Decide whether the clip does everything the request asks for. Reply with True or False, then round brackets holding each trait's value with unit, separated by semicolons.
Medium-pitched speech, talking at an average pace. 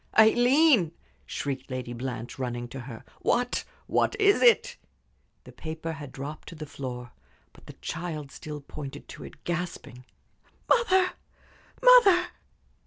False (155 Hz; 130 wpm)